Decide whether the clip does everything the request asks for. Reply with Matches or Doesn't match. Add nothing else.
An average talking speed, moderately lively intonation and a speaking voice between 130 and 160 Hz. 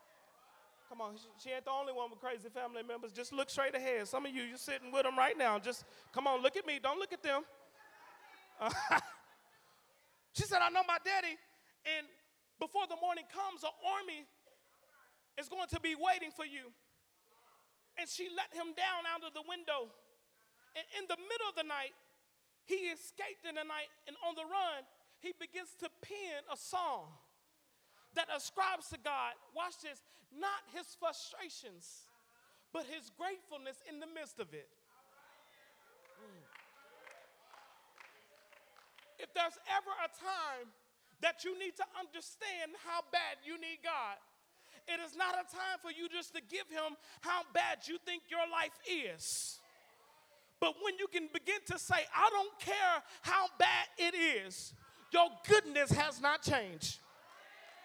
Doesn't match